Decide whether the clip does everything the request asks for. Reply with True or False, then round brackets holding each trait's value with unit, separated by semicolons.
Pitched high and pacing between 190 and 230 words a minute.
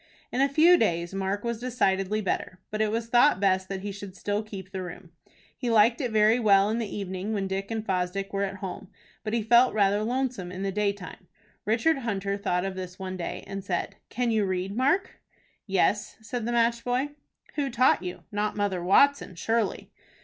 True (205 Hz; 200 wpm)